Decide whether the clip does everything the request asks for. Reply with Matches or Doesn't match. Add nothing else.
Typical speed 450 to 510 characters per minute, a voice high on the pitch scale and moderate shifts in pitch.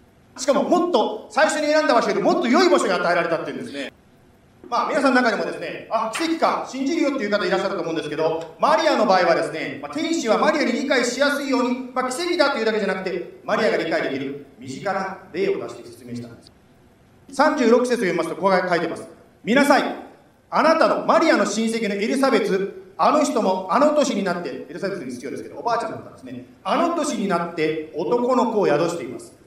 Doesn't match